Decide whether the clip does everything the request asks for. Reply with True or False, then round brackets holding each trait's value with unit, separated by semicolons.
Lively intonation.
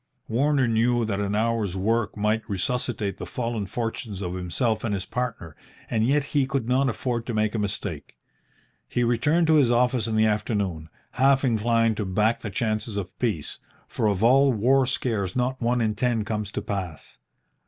False (3.1 semitones)